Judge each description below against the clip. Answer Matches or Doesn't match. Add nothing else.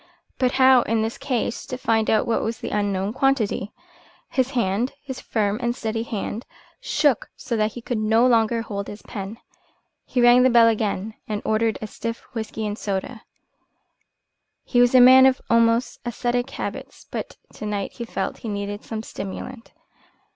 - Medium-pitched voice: Doesn't match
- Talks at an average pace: Matches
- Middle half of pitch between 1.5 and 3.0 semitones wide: Matches